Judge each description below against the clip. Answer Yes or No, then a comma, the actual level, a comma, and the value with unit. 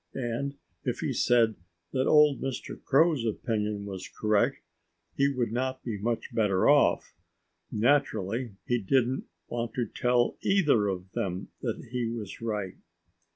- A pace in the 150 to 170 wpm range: No, average, 140 wpm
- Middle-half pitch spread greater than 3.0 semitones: Yes, average, 3.8 semitones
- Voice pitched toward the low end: Yes, low, 120 Hz